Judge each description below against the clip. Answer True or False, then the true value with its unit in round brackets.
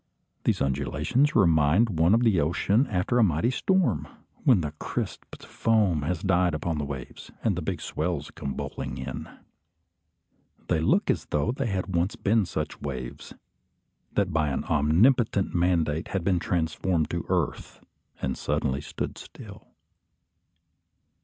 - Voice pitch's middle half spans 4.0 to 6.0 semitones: True (5.2 semitones)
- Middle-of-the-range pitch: False (85 Hz)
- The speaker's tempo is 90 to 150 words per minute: True (145 wpm)